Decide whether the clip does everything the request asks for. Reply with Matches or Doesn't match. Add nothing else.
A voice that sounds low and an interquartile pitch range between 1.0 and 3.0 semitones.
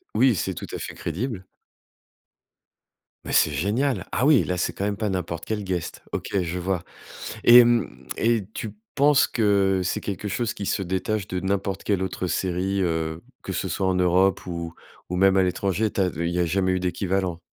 Matches